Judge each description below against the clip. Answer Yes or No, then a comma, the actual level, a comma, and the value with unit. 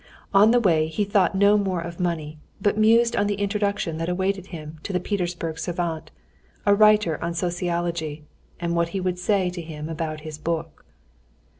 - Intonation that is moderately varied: Yes, average, 3.6 semitones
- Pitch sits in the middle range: Yes, medium, 175 Hz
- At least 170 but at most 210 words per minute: Yes, average, 180 wpm